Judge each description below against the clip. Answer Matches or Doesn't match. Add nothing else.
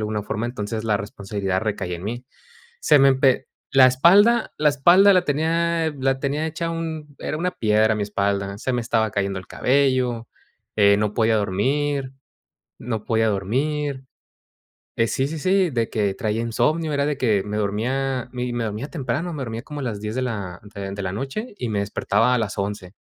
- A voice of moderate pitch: Doesn't match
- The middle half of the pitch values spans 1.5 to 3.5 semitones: Doesn't match